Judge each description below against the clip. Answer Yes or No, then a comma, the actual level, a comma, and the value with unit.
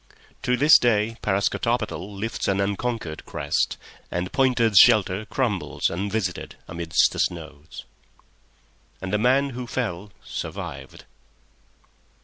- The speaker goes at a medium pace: No, slow, 110 wpm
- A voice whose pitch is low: Yes, low, 105 Hz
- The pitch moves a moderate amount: Yes, average, 4.6 semitones